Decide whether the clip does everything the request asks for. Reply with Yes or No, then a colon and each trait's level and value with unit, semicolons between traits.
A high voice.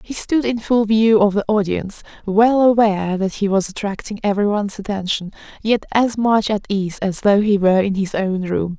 Yes: high, 205 Hz